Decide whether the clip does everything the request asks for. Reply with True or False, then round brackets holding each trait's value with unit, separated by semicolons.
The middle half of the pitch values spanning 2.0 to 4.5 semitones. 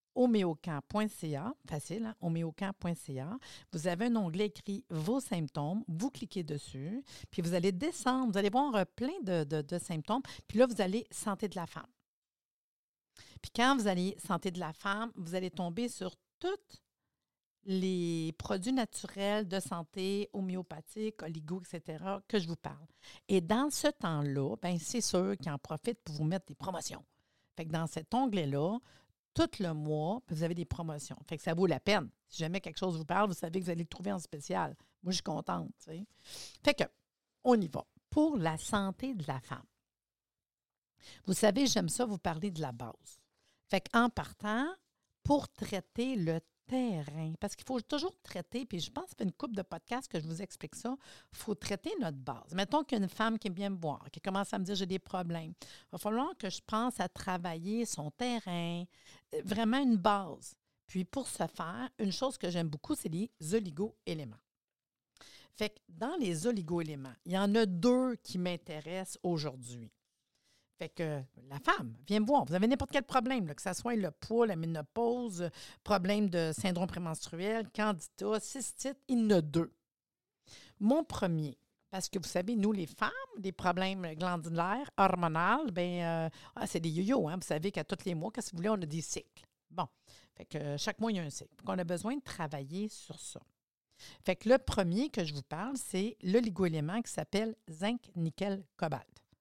False (5.0 semitones)